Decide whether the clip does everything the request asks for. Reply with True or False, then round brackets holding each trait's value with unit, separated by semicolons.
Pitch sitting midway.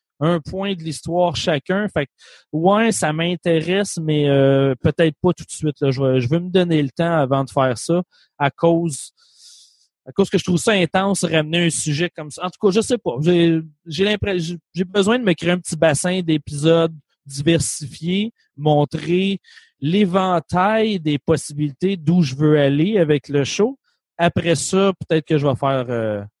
True (165 Hz)